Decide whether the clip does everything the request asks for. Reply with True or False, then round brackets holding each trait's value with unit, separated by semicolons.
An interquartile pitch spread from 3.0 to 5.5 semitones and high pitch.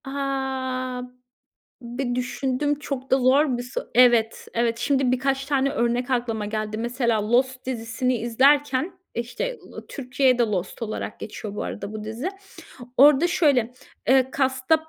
False (2.5 semitones; 255 Hz)